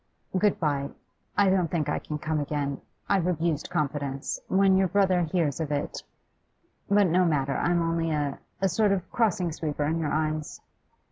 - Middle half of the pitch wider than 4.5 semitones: No, average, 3.9 semitones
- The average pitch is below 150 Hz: No, medium, 165 Hz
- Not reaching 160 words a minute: No, average, 175 wpm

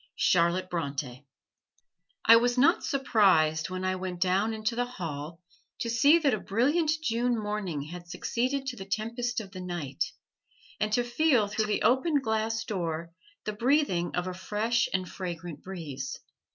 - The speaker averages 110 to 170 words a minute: Yes, average, 160 wpm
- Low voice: No, high, 210 Hz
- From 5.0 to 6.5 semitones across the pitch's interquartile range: Yes, wide, 5.4 semitones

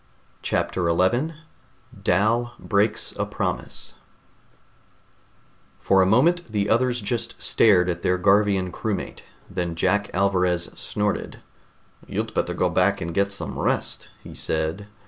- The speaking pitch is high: No, low, 100 Hz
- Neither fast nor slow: No, slow, 125 wpm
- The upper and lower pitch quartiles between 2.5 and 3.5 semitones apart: Yes, average, 3.1 semitones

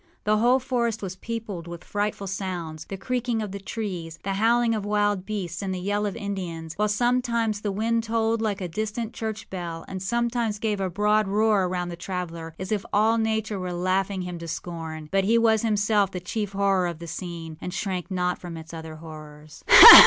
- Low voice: No, high, 195 Hz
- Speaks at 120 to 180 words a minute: No, average, 200 wpm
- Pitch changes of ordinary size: Yes, average, 3.7 semitones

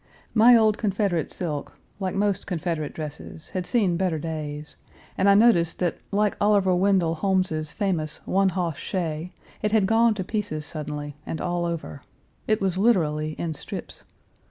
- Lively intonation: No, average, 4.4 semitones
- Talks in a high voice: No, medium, 180 Hz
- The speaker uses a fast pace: No, average, 155 wpm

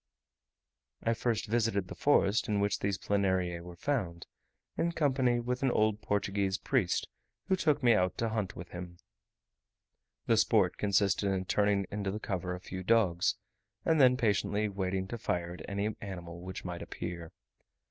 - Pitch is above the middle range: No, low, 100 Hz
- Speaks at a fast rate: No, average, 165 wpm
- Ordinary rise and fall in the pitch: Yes, average, 3.8 semitones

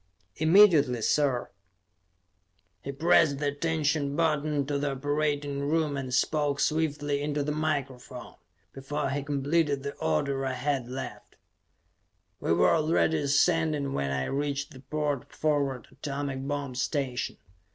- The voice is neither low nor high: Yes, medium, 145 Hz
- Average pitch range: No, narrow, 1.9 semitones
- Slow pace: Yes, slow, 130 wpm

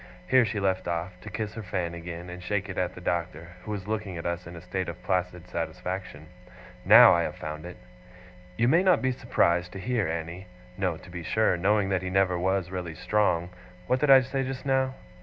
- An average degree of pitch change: Yes, average, 3.5 semitones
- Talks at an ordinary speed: No, fast, 220 wpm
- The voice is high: No, very low, 95 Hz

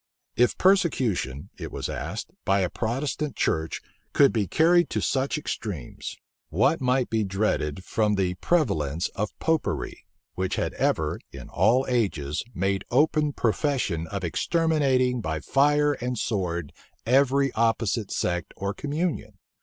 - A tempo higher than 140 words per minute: No, slow, 135 wpm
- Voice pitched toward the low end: Yes, low, 115 Hz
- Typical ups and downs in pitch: No, wide, 6.9 semitones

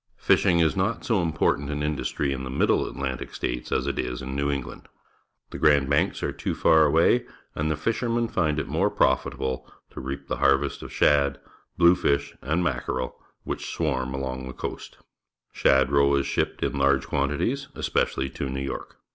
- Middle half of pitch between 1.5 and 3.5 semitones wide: Yes, average, 2.9 semitones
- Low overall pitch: Yes, very low, 70 Hz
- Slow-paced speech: No, average, 175 wpm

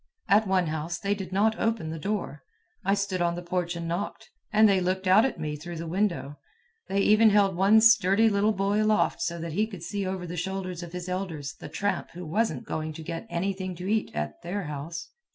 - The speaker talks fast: Yes, fast, 225 wpm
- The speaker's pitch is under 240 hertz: Yes, medium, 185 Hz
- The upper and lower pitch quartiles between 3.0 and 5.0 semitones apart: Yes, average, 3.3 semitones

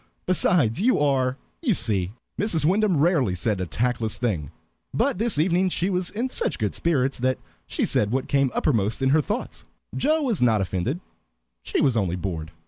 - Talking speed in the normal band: Yes, average, 180 wpm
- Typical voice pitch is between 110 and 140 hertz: Yes, low, 135 Hz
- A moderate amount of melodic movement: No, wide, 8.8 semitones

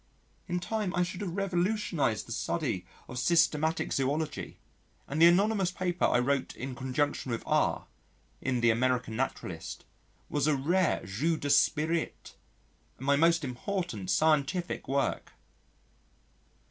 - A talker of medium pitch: Yes, medium, 150 Hz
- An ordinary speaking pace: No, slow, 130 wpm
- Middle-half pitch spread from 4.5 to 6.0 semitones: Yes, average, 5.0 semitones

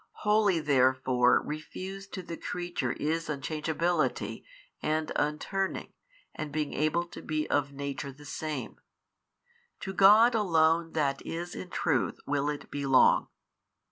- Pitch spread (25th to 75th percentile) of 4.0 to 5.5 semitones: No, average, 3.6 semitones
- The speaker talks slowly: Yes, slow, 130 wpm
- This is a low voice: No, medium, 155 Hz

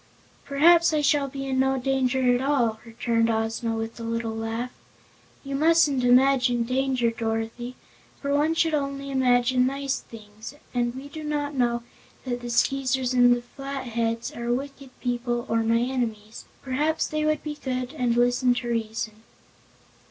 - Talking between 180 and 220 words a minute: No, average, 155 wpm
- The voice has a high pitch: Yes, very high, 250 Hz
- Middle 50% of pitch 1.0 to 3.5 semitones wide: Yes, average, 2.7 semitones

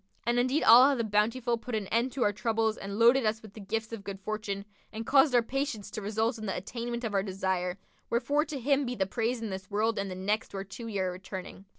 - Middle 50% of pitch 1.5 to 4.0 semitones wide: Yes, average, 3.3 semitones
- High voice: Yes, high, 220 Hz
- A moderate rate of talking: No, fast, 245 wpm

